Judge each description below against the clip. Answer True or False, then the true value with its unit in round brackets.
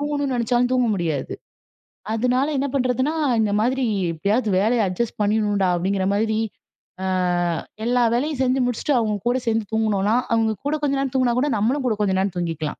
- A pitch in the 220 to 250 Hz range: True (230 Hz)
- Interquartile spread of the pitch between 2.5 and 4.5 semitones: True (3.9 semitones)